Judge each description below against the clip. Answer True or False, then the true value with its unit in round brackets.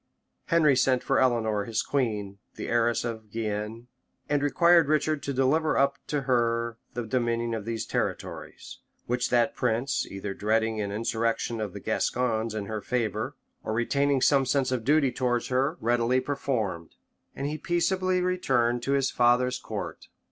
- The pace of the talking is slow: False (160 wpm)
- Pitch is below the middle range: True (120 Hz)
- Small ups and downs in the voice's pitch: False (3.5 semitones)